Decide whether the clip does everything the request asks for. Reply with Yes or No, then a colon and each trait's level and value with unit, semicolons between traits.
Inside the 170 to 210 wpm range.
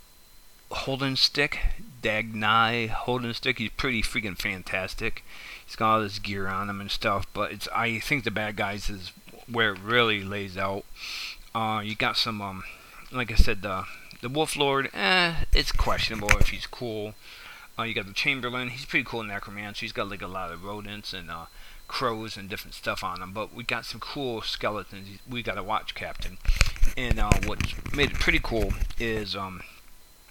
Yes: average, 185 wpm